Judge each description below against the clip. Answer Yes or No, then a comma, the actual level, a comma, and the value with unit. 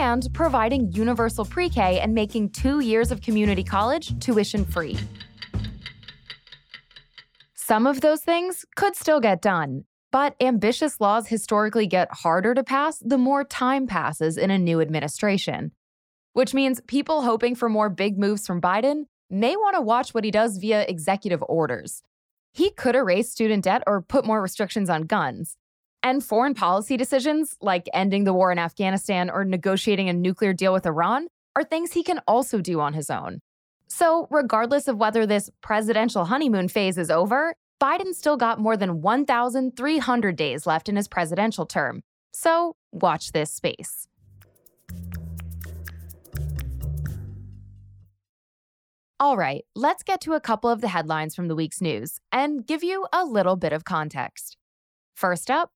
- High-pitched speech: Yes, high, 210 Hz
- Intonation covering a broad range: Yes, wide, 7.5 semitones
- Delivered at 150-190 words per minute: Yes, average, 155 wpm